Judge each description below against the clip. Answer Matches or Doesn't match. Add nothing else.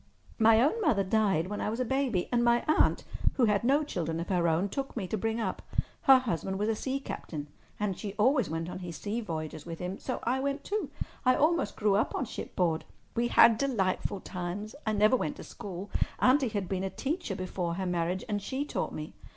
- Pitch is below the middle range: Doesn't match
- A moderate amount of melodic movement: Doesn't match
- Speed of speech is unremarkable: Doesn't match